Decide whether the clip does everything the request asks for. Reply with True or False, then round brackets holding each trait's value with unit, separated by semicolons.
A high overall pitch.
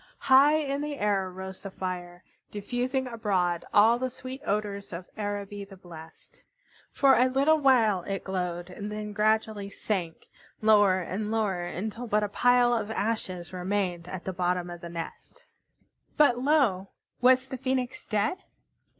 True (205 Hz)